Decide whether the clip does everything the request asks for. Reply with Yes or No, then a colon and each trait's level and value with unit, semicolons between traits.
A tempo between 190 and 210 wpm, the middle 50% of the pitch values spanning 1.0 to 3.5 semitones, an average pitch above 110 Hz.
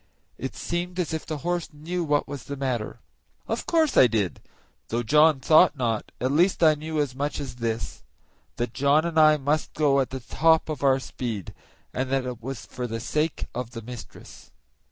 No: average, 195 wpm; average, 4.3 semitones; medium, 140 Hz